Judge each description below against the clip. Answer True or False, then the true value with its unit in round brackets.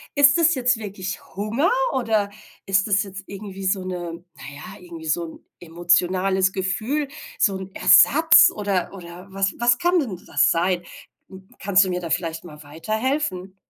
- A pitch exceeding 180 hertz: True (190 Hz)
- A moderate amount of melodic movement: True (3.4 semitones)